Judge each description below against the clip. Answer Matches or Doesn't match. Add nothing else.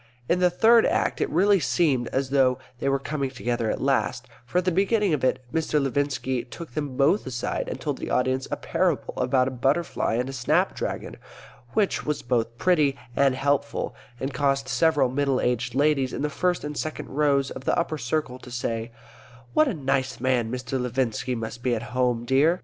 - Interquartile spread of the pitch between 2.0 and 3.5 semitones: Matches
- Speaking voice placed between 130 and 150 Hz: Matches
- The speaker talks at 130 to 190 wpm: Doesn't match